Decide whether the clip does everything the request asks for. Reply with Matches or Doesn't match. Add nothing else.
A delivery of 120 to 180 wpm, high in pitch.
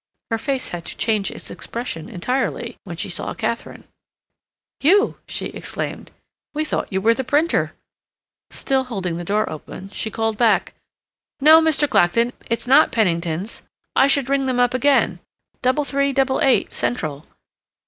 Matches